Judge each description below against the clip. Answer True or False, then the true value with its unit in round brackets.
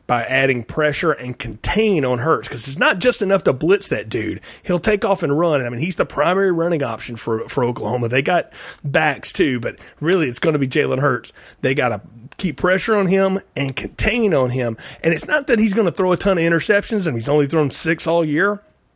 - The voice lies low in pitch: False (165 Hz)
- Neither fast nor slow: False (230 wpm)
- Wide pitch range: True (6.8 semitones)